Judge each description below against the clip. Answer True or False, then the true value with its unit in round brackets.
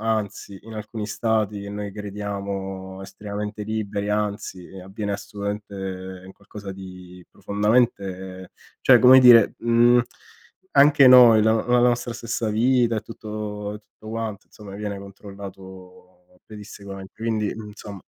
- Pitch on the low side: True (105 Hz)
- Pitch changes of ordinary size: False (2.2 semitones)